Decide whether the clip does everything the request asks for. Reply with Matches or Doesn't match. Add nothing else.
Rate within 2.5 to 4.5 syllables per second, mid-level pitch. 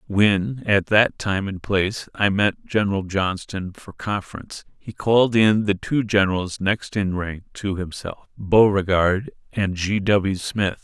Doesn't match